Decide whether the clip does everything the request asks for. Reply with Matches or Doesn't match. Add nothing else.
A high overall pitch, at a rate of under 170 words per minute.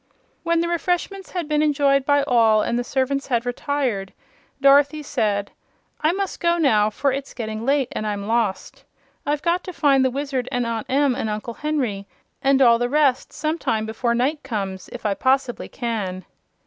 Doesn't match